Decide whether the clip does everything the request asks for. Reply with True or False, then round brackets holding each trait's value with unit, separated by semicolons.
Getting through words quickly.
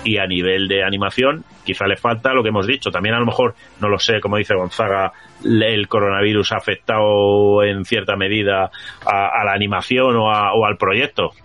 True (200 wpm)